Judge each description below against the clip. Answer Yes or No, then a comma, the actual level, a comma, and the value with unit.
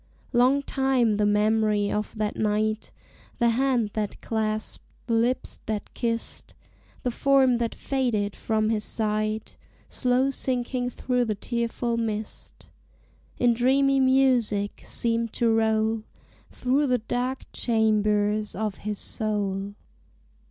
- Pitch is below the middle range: No, high, 225 Hz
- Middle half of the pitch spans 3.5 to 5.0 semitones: No, average, 2.7 semitones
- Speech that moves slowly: Yes, slow, 120 wpm